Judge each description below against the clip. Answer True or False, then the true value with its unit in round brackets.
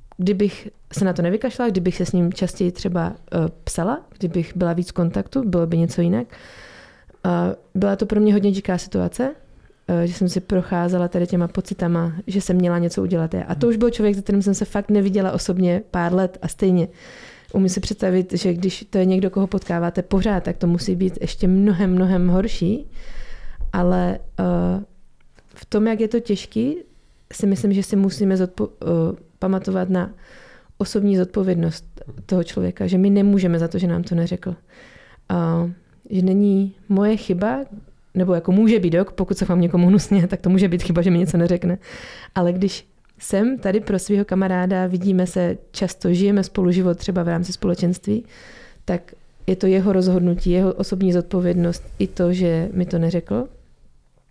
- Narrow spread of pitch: True (2.3 semitones)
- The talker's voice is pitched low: False (185 Hz)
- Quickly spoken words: True (180 wpm)